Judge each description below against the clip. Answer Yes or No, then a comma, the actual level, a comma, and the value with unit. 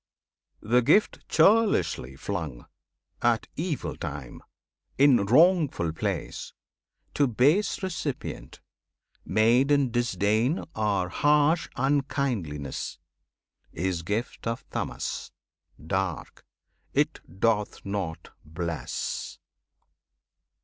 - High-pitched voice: No, low, 115 Hz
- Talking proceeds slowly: Yes, slow, 80 wpm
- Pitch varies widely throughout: Yes, wide, 7.9 semitones